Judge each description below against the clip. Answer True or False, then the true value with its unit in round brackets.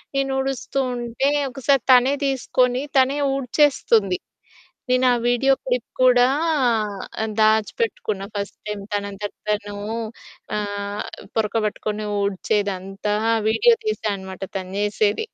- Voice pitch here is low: False (220 Hz)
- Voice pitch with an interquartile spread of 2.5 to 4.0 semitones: False (4.4 semitones)